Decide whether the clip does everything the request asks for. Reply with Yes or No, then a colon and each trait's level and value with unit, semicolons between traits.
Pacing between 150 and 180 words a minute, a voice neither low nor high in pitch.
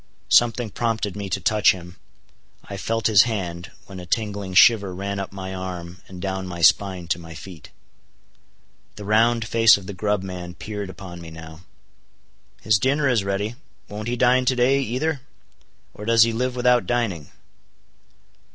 No: average, 170 wpm; low, 100 Hz